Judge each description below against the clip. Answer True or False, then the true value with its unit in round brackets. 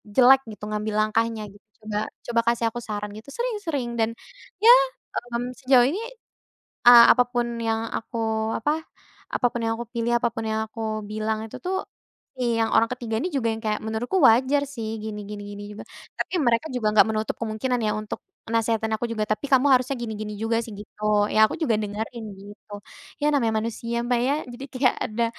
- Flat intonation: True (2.3 semitones)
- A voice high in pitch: True (225 Hz)